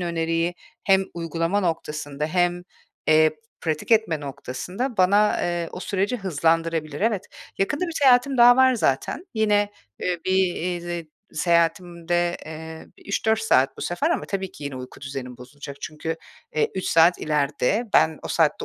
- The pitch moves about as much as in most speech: Yes, average, 4.2 semitones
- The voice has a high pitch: No, medium, 175 Hz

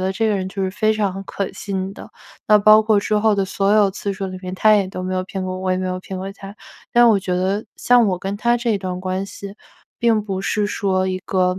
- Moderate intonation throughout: No, narrow, 2.1 semitones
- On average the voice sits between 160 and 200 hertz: Yes, high, 195 Hz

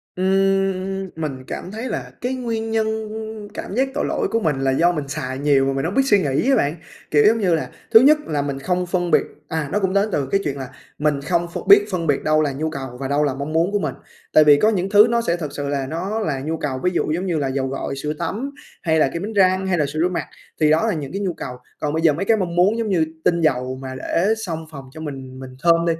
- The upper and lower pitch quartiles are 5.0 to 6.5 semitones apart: Yes, wide, 5.5 semitones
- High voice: No, medium, 160 Hz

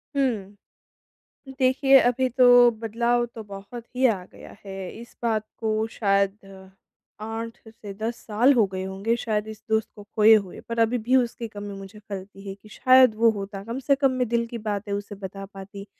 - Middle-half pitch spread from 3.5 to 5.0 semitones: No, average, 2.9 semitones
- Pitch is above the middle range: Yes, high, 220 Hz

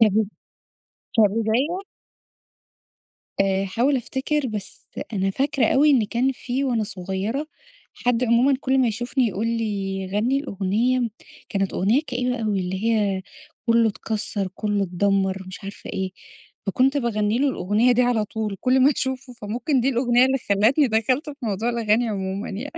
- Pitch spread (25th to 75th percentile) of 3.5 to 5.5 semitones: Yes, average, 4.1 semitones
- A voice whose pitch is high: Yes, high, 225 Hz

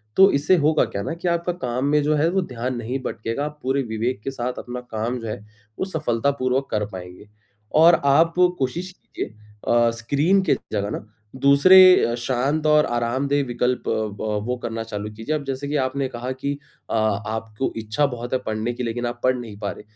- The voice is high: No, low, 125 Hz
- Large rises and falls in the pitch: No, average, 4.3 semitones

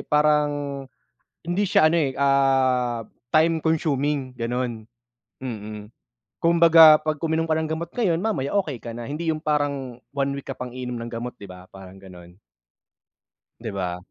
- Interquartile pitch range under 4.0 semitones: No, average, 5.0 semitones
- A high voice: No, medium, 140 Hz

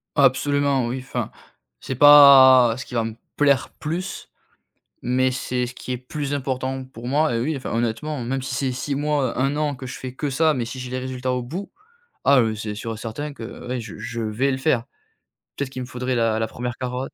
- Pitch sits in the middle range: No, low, 130 Hz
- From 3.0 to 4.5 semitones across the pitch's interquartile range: No, narrow, 2.4 semitones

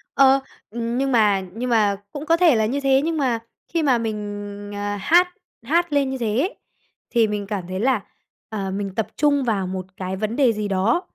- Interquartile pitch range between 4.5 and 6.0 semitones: Yes, average, 5.0 semitones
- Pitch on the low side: No, high, 225 Hz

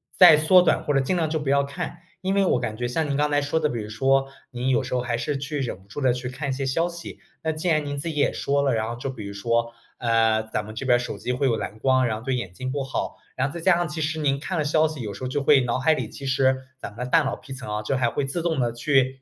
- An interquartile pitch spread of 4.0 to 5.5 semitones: No, average, 3.6 semitones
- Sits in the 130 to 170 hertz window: Yes, low, 135 Hz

